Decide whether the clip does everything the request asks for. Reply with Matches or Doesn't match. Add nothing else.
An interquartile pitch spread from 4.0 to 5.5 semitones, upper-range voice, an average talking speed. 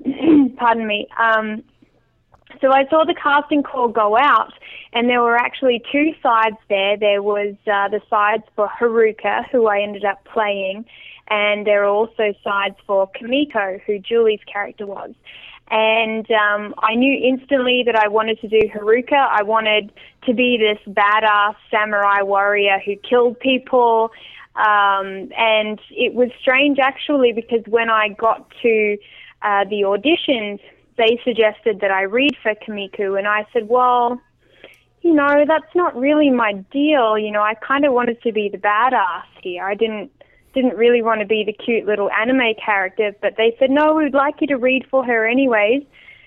Doesn't match